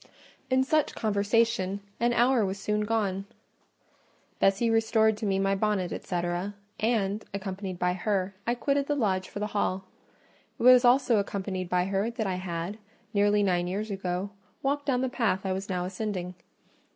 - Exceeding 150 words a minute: Yes, average, 165 wpm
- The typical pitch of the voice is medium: No, high, 205 Hz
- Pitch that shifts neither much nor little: Yes, average, 3.2 semitones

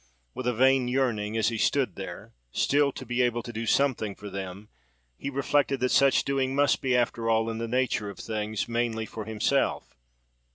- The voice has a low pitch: Yes, low, 120 Hz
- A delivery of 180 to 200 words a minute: Yes, average, 195 wpm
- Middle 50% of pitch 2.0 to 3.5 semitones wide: Yes, average, 3.2 semitones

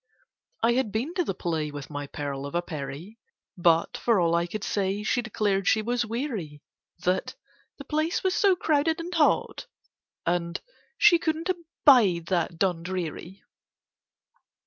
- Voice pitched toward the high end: Yes, high, 195 Hz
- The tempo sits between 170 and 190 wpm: No, average, 150 wpm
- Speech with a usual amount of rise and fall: No, wide, 8.7 semitones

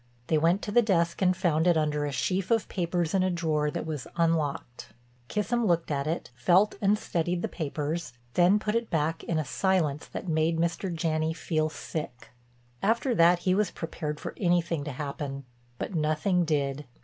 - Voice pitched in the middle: Yes, medium, 165 Hz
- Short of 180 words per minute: No, average, 185 wpm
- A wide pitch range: No, average, 3.2 semitones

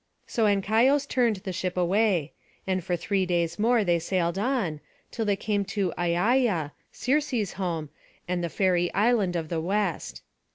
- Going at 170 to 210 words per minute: No, average, 160 wpm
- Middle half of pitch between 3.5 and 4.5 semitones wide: Yes, average, 4.0 semitones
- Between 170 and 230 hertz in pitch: Yes, high, 190 Hz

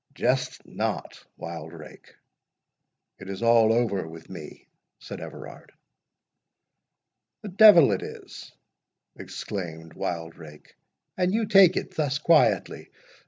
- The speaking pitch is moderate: No, low, 110 Hz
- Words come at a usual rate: No, slow, 100 wpm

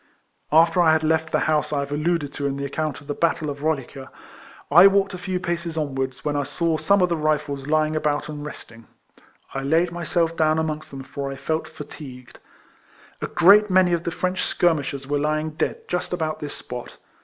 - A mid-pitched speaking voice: Yes, medium, 155 Hz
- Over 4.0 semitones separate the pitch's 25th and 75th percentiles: No, average, 2.9 semitones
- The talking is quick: Yes, fast, 210 wpm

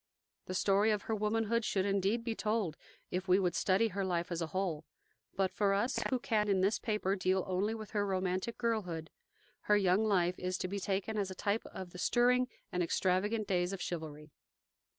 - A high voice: Yes, high, 195 Hz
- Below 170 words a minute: No, average, 200 wpm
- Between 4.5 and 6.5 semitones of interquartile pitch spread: No, average, 2.8 semitones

